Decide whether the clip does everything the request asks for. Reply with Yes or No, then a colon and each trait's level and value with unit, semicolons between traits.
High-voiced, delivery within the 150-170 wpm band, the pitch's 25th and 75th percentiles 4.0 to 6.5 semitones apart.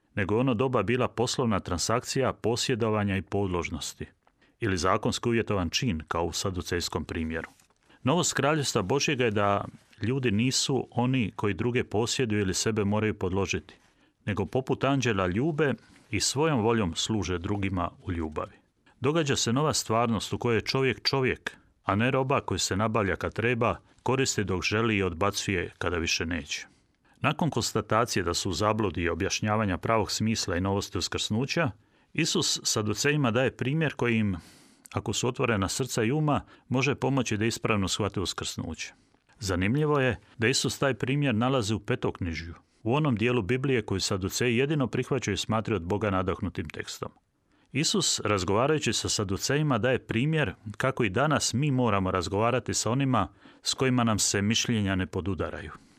No: low, 110 Hz; average, 155 wpm; average, 4.5 semitones